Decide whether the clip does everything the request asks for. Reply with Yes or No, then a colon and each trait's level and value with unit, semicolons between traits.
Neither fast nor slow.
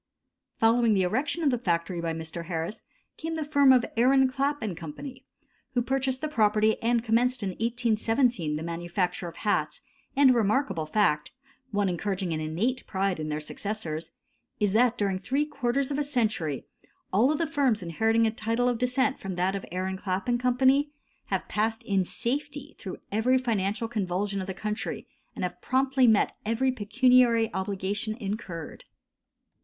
Yes: average, 170 wpm